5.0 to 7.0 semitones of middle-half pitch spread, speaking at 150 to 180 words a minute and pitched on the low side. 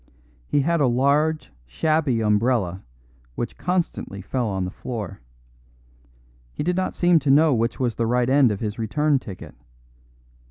Yes: wide, 5.6 semitones; average, 155 wpm; low, 125 Hz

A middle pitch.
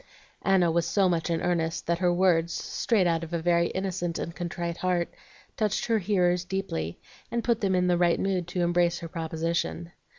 Yes: medium, 175 Hz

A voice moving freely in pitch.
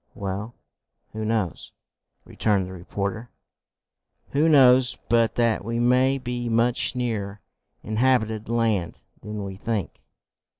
No: average, 2.9 semitones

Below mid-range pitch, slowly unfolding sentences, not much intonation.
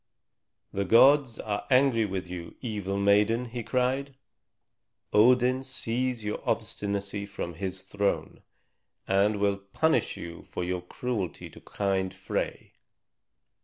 No: low, 105 Hz; slow, 120 wpm; average, 4.3 semitones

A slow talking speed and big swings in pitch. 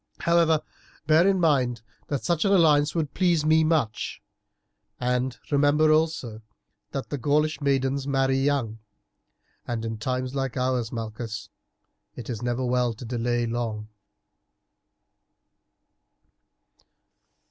No: slow, 115 wpm; average, 4.3 semitones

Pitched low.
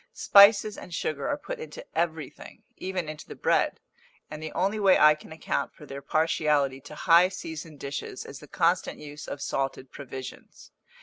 No: medium, 155 Hz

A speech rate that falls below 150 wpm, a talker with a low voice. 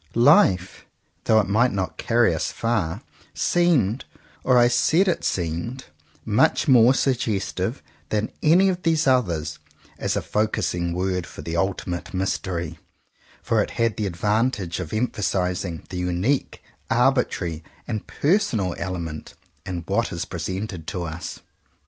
Yes: slow, 135 wpm; low, 100 Hz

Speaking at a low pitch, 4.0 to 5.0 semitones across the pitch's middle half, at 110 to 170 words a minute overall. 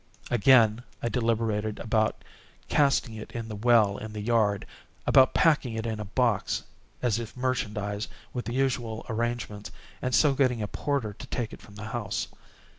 No: low, 115 Hz; narrow, 2.6 semitones; average, 165 wpm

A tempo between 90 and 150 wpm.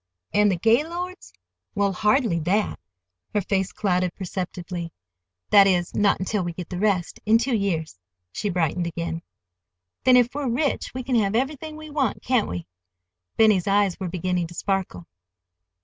Yes: average, 145 wpm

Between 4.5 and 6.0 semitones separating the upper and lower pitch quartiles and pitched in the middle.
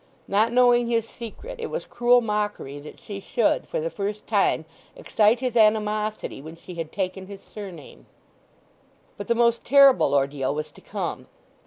No: average, 5.0 semitones; high, 210 Hz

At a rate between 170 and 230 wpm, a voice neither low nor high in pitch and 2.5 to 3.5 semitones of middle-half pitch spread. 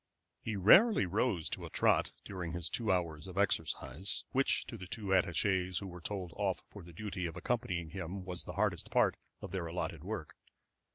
No: average, 190 wpm; very low, 95 Hz; average, 3.0 semitones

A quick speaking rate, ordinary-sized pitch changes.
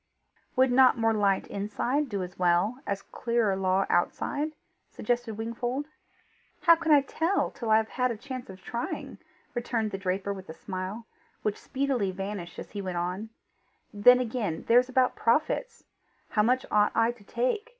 No: average, 170 wpm; average, 4.4 semitones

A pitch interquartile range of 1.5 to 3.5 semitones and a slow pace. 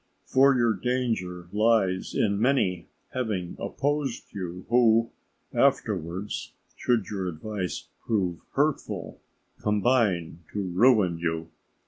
No: average, 5.0 semitones; slow, 100 wpm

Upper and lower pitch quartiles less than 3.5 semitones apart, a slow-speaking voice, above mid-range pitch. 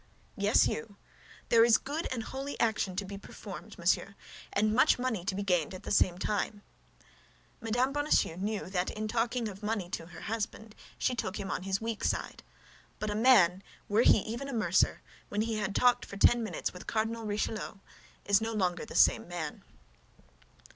No: average, 2.9 semitones; average, 185 wpm; high, 215 Hz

